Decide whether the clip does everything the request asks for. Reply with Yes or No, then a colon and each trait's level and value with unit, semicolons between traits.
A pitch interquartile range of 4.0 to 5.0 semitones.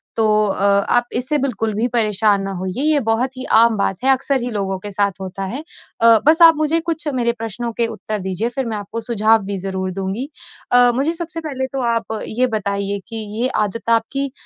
Yes: average, 4.5 semitones